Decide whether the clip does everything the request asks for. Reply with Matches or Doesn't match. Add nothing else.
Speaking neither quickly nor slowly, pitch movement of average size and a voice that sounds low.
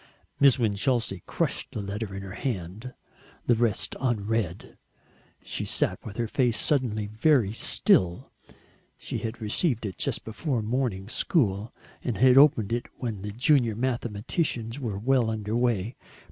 Matches